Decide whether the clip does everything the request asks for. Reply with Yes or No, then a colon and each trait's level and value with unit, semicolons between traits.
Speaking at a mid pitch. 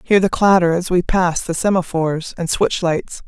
Yes: medium, 175 Hz